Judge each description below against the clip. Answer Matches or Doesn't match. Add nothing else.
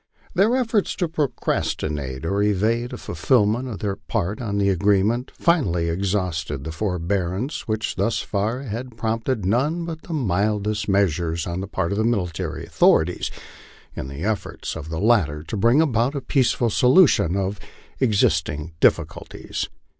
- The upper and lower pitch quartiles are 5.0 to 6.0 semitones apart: Matches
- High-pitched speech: Doesn't match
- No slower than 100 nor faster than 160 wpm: Matches